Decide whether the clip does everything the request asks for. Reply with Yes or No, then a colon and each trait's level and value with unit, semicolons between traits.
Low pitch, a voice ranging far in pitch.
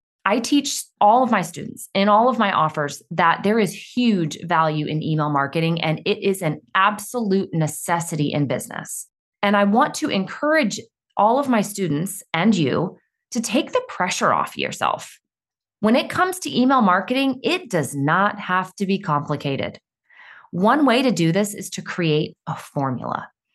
No: high, 195 Hz; wide, 6.2 semitones